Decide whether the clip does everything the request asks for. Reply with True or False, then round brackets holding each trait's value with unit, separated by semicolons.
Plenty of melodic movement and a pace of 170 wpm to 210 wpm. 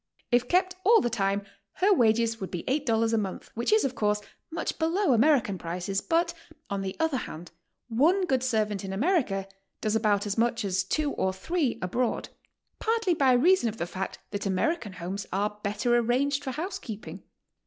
True (7.4 semitones; 180 wpm)